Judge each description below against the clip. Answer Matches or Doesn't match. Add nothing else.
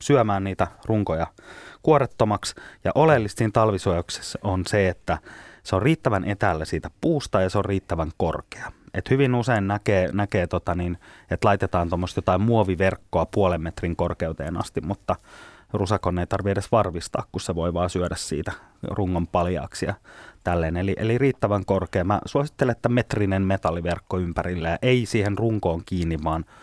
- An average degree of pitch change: Matches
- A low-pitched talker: Matches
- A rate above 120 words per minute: Matches